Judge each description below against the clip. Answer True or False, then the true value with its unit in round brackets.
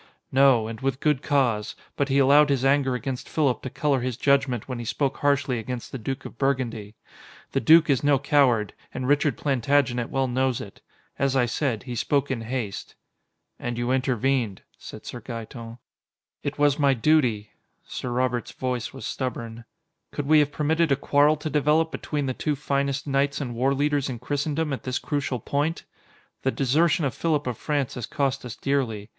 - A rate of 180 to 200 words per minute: True (185 wpm)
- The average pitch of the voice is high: False (135 Hz)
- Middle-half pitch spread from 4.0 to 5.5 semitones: False (2.8 semitones)